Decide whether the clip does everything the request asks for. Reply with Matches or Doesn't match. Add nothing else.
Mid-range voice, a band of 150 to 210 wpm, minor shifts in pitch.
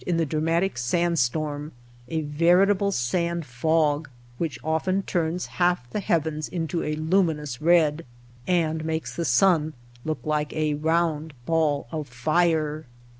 Doesn't match